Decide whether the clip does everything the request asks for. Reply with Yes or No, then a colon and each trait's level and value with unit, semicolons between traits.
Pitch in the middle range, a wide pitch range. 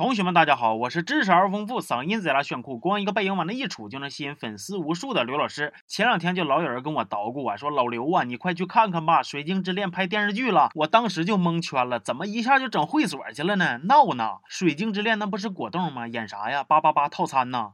Yes: medium, 175 Hz; wide, 6.4 semitones